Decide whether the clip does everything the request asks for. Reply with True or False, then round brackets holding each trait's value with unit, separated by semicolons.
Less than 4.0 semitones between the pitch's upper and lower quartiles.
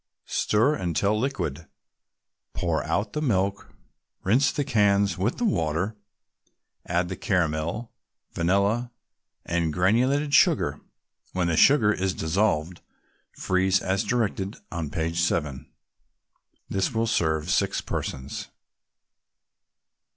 False (4.7 semitones)